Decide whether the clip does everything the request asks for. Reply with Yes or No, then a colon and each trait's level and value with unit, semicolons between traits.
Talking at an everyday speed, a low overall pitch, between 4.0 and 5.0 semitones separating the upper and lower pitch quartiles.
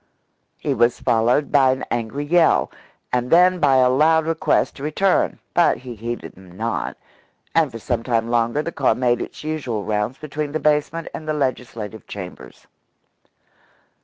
Yes: average, 160 wpm; low, 130 Hz; average, 4.7 semitones